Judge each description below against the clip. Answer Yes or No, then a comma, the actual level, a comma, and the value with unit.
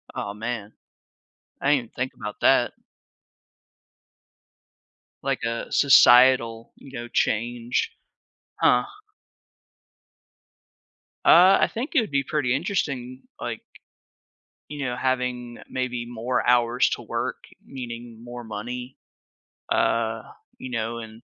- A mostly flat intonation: Yes, narrow, 2.0 semitones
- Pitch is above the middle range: No, low, 120 Hz